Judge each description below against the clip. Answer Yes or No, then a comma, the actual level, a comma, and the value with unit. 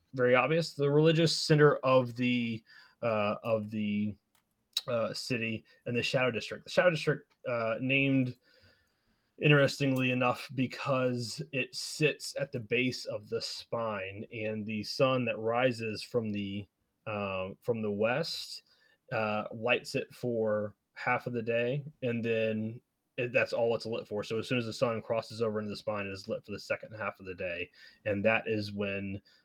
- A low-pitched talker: Yes, low, 115 Hz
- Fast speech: No, average, 170 wpm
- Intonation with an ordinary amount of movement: Yes, average, 3.3 semitones